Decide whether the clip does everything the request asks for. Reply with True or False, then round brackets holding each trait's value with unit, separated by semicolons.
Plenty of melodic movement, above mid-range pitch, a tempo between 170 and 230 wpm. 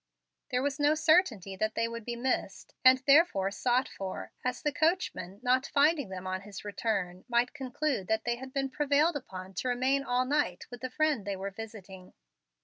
True (6.0 semitones; 245 Hz; 190 wpm)